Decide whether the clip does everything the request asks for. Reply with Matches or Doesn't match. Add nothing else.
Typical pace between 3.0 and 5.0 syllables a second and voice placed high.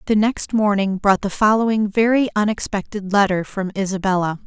Doesn't match